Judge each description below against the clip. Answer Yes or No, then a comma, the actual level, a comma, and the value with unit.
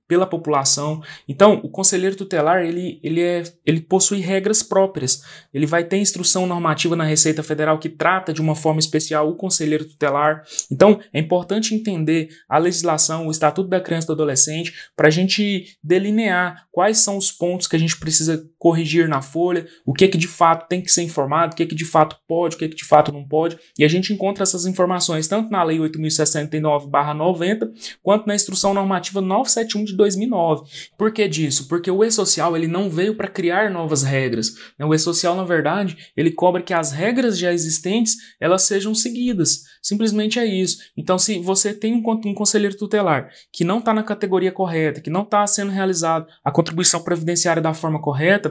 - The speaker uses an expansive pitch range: No, average, 3.8 semitones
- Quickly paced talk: Yes, fast, 190 wpm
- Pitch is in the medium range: Yes, medium, 175 Hz